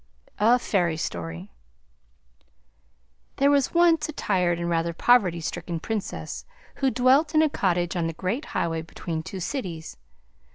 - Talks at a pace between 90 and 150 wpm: Yes, average, 140 wpm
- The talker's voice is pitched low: No, medium, 185 Hz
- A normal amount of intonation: No, wide, 7.6 semitones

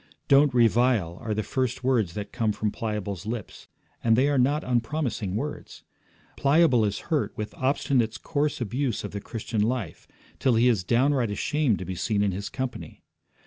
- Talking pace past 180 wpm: No, average, 175 wpm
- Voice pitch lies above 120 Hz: No, low, 115 Hz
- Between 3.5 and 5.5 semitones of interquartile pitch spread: Yes, average, 4.1 semitones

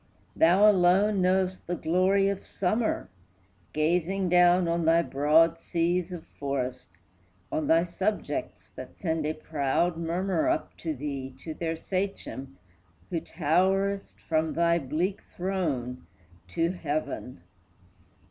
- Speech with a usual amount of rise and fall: Yes, average, 3.1 semitones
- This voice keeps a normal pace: No, slow, 120 wpm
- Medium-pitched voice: Yes, medium, 170 Hz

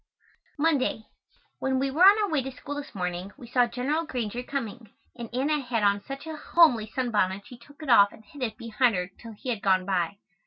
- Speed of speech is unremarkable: No, fast, 220 wpm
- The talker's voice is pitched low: No, high, 245 Hz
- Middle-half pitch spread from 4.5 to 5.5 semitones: Yes, average, 4.9 semitones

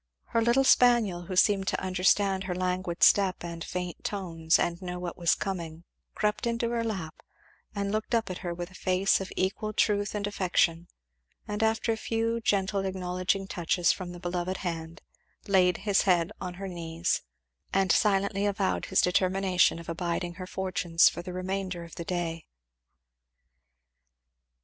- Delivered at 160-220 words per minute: Yes, average, 165 wpm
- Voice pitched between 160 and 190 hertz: Yes, medium, 185 Hz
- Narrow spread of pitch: Yes, narrow, 2.3 semitones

